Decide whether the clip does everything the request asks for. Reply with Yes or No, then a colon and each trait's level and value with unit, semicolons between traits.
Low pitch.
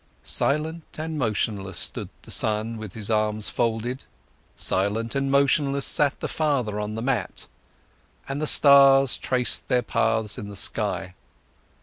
Yes: low, 120 Hz